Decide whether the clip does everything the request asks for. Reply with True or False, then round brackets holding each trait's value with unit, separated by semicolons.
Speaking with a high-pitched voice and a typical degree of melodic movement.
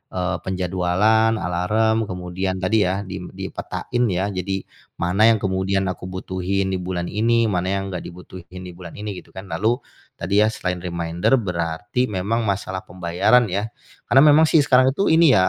False (95 Hz; 3.2 semitones)